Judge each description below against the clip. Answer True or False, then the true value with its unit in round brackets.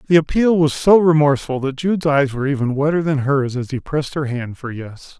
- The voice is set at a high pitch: False (145 Hz)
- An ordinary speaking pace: False (230 wpm)